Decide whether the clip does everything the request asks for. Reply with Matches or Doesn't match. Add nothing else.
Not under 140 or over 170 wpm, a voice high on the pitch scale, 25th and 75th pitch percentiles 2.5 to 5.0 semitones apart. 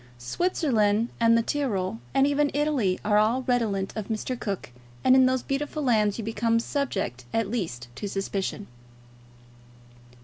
Matches